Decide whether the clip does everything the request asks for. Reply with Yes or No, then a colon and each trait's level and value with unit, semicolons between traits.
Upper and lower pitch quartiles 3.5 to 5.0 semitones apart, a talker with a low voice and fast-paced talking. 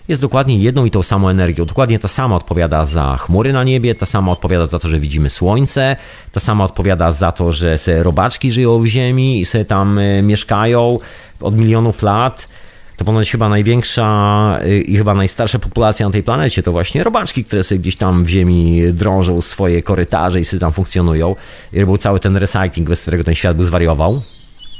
Yes: average, 4.6 semitones; low, 100 Hz; fast, 190 wpm